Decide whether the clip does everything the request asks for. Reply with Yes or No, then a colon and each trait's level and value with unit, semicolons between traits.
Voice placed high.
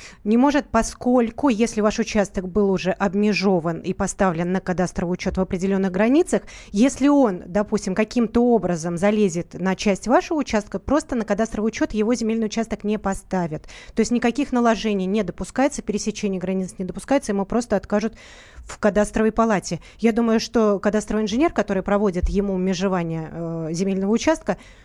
Yes: high, 210 Hz